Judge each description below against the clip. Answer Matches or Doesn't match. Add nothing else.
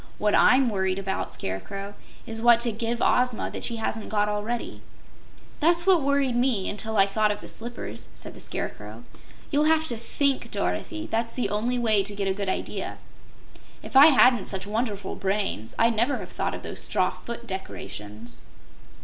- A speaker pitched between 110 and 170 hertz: Doesn't match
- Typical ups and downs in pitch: Matches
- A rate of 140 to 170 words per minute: Doesn't match